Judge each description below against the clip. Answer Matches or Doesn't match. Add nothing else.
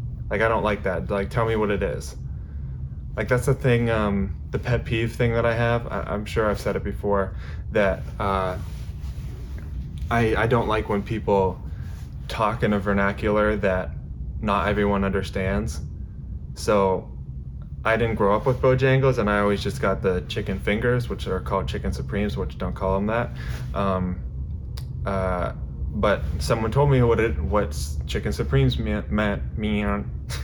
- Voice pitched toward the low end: Matches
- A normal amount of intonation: Doesn't match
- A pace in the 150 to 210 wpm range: Matches